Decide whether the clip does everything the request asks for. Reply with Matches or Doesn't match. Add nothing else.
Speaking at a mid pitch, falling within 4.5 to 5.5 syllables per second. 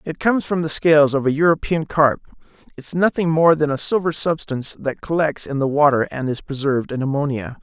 Doesn't match